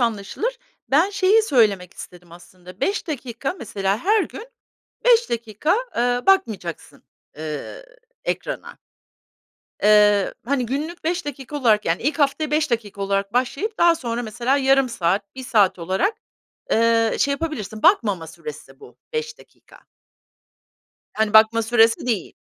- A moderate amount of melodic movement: No, wide, 7.2 semitones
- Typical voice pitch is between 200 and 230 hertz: No, high, 240 Hz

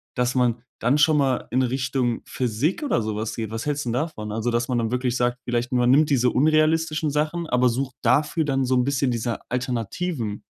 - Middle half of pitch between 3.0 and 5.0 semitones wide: Yes, average, 3.5 semitones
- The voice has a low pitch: Yes, low, 125 Hz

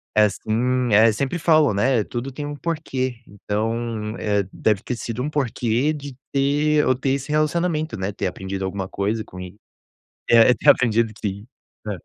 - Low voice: Yes, low, 120 Hz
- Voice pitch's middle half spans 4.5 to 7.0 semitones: Yes, average, 4.8 semitones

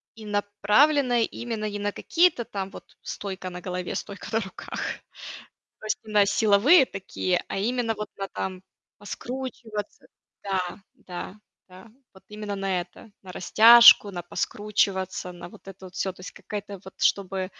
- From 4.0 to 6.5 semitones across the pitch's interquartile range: No, average, 2.8 semitones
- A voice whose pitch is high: Yes, high, 205 Hz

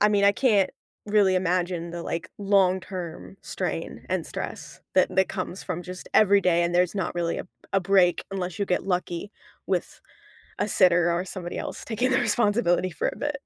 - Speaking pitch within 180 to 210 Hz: Yes, medium, 185 Hz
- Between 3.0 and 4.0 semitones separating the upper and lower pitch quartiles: No, narrow, 2.4 semitones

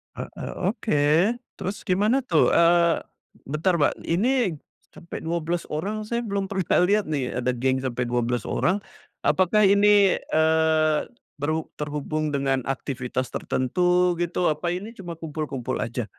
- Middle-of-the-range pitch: Yes, medium, 160 Hz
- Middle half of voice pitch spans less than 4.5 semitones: No, wide, 5.5 semitones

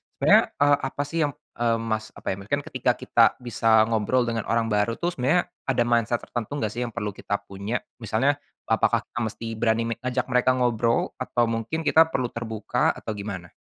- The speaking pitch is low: Yes, low, 115 Hz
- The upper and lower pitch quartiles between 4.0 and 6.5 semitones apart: No, average, 2.7 semitones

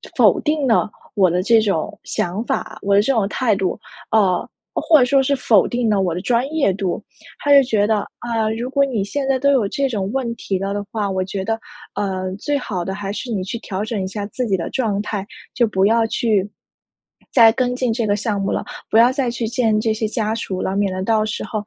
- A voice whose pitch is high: Yes, high, 220 Hz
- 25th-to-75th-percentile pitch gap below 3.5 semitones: No, average, 3.8 semitones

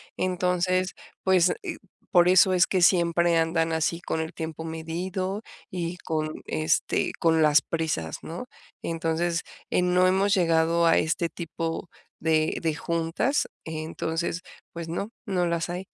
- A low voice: No, medium, 170 Hz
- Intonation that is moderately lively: No, narrow, 1.9 semitones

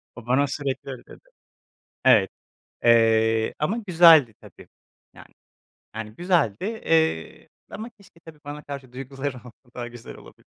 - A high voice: No, low, 135 Hz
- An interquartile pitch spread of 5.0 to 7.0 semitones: Yes, wide, 5.5 semitones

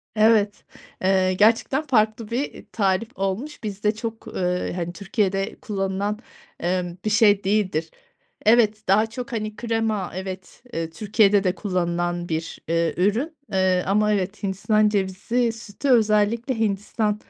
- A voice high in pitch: Yes, high, 205 Hz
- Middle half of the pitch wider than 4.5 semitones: No, average, 2.8 semitones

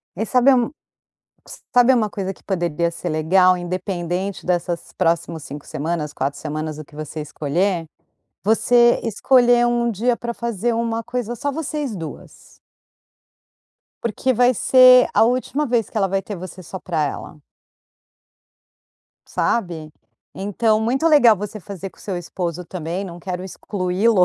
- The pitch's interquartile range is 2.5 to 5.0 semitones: No, wide, 5.6 semitones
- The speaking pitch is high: Yes, high, 195 Hz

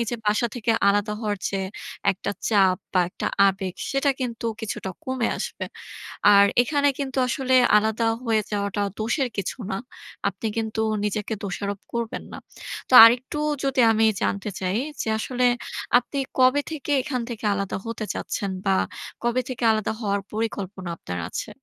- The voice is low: No, high, 220 Hz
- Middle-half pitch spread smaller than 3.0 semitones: No, average, 3.8 semitones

